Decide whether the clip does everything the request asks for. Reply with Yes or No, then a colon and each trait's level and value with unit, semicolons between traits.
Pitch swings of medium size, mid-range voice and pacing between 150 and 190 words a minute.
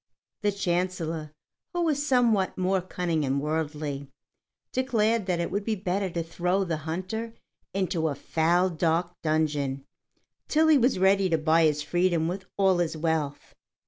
Yes: average, 3.7 semitones; medium, 175 Hz; average, 155 wpm